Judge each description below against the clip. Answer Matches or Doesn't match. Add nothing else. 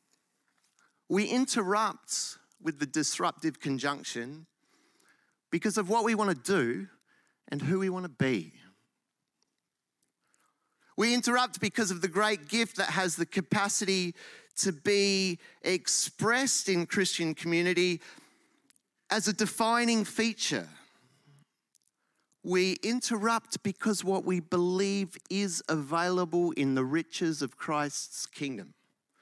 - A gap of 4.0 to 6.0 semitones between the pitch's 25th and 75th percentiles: Matches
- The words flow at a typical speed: Doesn't match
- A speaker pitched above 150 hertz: Matches